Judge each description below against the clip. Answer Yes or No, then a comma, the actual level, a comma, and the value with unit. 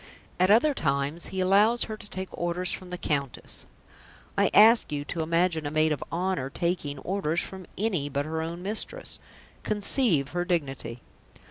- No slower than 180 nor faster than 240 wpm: No, average, 165 wpm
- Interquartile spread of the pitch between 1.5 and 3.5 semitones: No, average, 4.3 semitones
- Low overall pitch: No, medium, 175 Hz